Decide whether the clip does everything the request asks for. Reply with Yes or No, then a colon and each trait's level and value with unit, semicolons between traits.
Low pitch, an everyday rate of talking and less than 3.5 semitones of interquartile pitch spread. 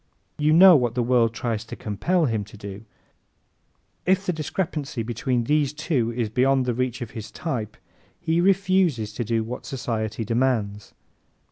No: low, 125 Hz; average, 160 wpm; average, 5.3 semitones